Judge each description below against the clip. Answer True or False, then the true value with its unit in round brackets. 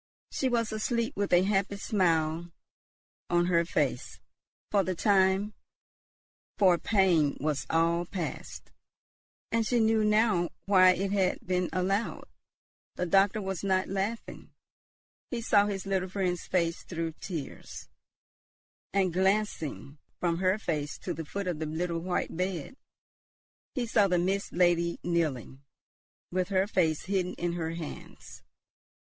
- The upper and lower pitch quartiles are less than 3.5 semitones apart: True (2.8 semitones)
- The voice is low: False (185 Hz)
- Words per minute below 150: True (135 wpm)